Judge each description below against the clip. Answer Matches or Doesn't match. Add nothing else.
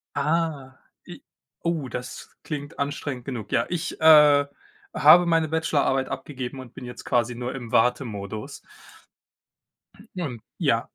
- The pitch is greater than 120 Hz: Matches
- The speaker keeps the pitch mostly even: Doesn't match